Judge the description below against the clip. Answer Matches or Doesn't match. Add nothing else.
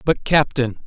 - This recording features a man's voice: Matches